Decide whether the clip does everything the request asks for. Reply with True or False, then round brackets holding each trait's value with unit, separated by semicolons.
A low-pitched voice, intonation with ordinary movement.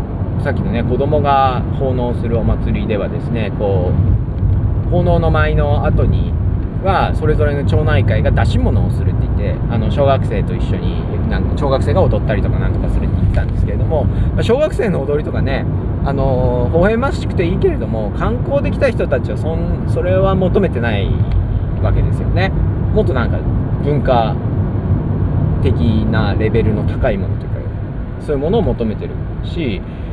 True (105 Hz; 3.4 semitones)